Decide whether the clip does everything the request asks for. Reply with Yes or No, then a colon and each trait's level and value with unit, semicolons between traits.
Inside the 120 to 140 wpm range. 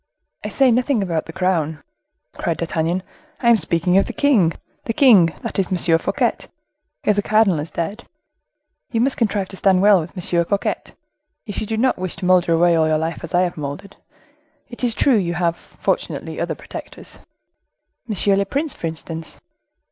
No: average, 185 wpm